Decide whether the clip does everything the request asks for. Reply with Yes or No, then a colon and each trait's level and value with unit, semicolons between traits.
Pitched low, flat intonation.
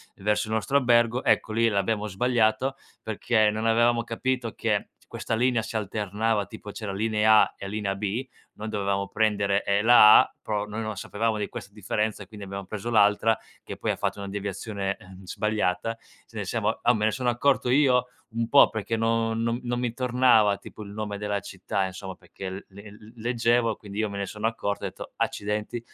Yes: low, 110 Hz; narrow, 2.2 semitones